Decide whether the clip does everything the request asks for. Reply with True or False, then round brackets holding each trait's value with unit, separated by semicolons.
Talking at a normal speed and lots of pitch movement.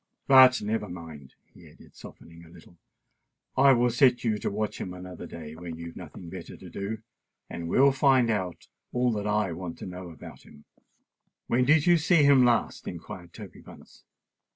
True (180 wpm; 6.6 semitones)